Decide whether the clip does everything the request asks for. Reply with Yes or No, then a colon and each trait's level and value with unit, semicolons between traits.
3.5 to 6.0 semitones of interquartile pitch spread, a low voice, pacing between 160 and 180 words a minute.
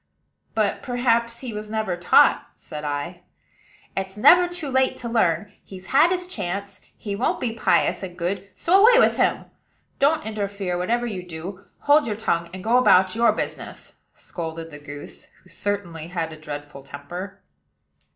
No: average, 5.3 semitones; high, 200 Hz; average, 165 wpm